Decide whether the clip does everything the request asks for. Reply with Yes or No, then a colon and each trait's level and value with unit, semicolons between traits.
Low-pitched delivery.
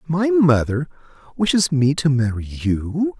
Yes: low, 130 Hz